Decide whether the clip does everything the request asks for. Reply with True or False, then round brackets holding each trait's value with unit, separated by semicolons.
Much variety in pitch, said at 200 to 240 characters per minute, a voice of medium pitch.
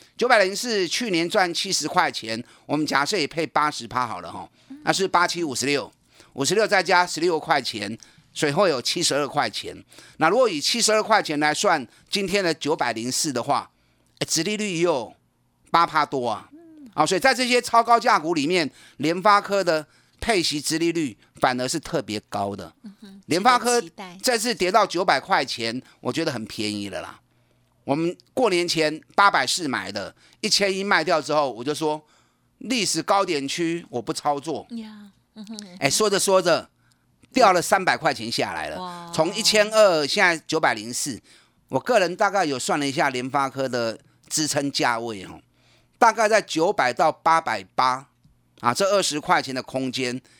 False (6.7 semitones; 255 characters per minute; 165 Hz)